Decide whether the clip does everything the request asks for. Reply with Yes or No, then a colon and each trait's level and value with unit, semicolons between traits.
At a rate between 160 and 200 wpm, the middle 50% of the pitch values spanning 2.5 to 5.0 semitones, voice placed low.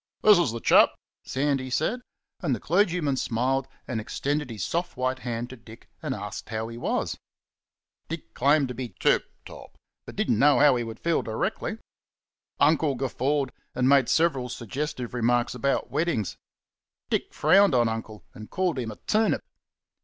Yes: average, 165 wpm; average, 4.0 semitones; low, 130 Hz